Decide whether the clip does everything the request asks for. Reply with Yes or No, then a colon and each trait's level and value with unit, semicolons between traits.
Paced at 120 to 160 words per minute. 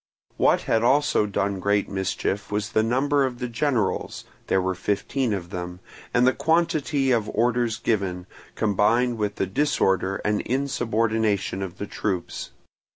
Yes: average, 150 wpm